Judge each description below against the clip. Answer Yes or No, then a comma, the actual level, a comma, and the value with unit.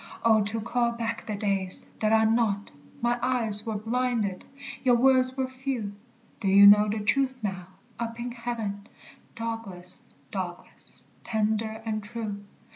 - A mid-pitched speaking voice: No, high, 220 Hz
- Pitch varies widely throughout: No, average, 2.7 semitones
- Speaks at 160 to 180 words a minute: No, average, 145 wpm